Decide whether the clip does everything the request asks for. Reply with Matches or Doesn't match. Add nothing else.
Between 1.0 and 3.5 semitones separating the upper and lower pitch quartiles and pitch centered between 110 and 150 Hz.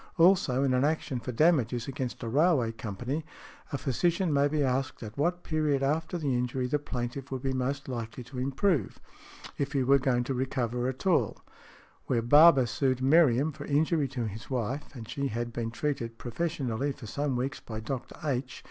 Matches